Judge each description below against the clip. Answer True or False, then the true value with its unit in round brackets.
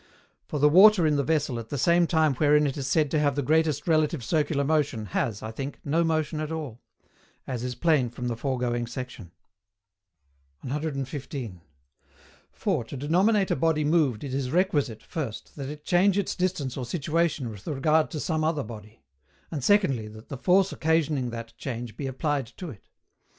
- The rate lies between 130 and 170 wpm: False (180 wpm)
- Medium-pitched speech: True (145 Hz)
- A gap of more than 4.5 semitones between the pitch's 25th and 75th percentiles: False (4.2 semitones)